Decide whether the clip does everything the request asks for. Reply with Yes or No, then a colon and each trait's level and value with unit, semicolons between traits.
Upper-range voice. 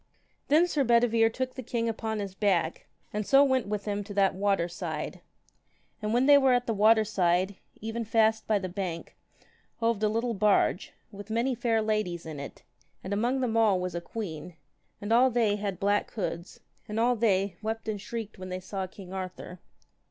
Yes: high, 210 Hz